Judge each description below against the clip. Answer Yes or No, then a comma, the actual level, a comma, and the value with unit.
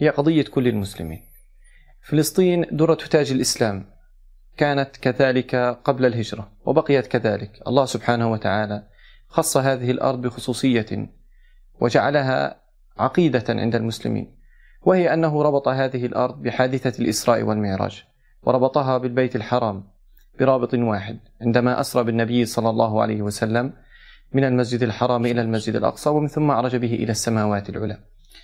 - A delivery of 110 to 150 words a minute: Yes, average, 120 wpm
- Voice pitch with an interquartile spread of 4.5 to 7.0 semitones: No, average, 3.3 semitones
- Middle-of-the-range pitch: No, low, 125 Hz